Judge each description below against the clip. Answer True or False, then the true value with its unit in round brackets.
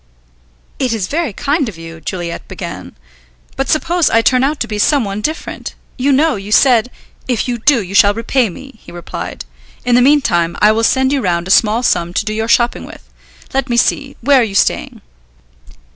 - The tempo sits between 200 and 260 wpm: True (205 wpm)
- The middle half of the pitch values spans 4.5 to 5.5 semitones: True (5.1 semitones)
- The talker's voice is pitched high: True (235 Hz)